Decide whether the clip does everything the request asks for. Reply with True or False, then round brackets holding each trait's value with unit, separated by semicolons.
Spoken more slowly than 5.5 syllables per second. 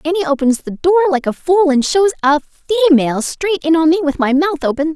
False (6.6 syllables/s)